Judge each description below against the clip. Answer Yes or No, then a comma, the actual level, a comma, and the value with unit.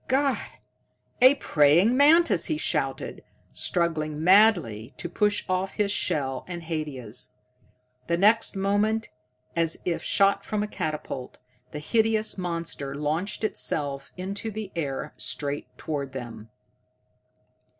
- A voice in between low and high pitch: Yes, medium, 175 Hz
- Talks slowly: Yes, slow, 120 wpm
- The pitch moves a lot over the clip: Yes, wide, 6.1 semitones